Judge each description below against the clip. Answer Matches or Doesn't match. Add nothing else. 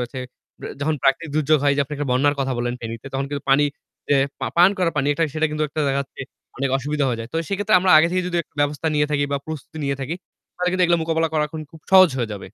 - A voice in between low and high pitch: Matches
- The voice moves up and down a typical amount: Matches